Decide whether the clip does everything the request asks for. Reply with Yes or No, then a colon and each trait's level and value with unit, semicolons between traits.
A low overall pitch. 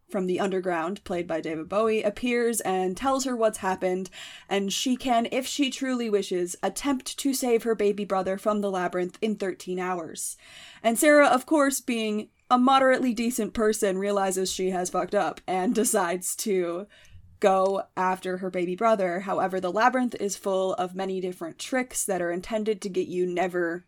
No: high, 195 Hz